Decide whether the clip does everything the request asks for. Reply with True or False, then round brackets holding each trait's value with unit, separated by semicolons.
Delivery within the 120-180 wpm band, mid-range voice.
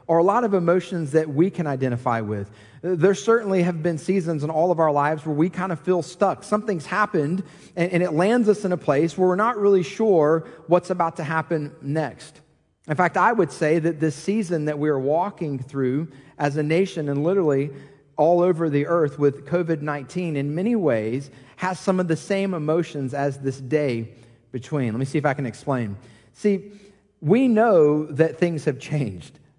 False (195 wpm; 160 Hz)